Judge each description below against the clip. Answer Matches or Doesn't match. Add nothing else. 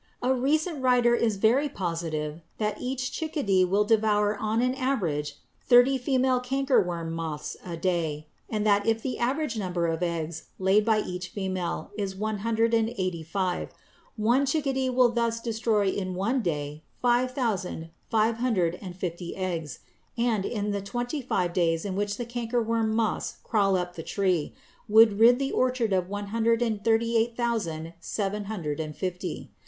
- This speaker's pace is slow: Doesn't match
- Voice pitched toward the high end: Matches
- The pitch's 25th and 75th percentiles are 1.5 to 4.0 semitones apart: Doesn't match